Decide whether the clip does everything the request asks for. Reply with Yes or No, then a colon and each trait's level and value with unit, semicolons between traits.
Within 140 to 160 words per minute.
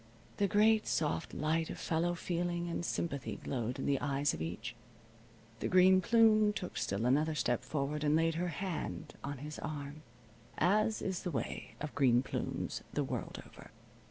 No: average, 170 wpm